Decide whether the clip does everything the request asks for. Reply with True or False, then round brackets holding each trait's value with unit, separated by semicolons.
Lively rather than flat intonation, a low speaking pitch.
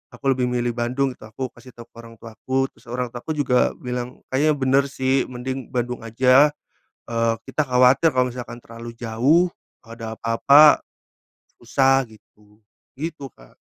False (2.4 semitones; 125 Hz)